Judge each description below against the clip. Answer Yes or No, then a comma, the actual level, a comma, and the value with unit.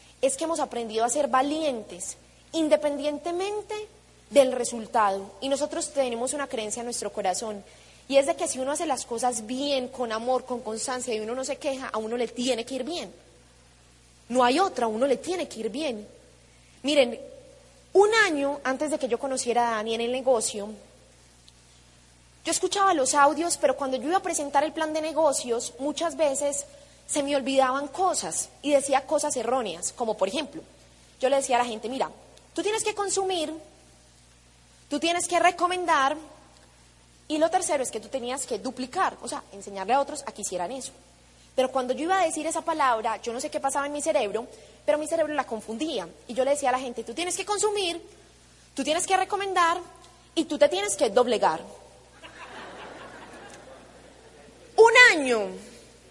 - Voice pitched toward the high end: Yes, very high, 270 Hz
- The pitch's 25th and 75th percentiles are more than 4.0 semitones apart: Yes, wide, 5.4 semitones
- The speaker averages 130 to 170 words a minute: No, average, 185 wpm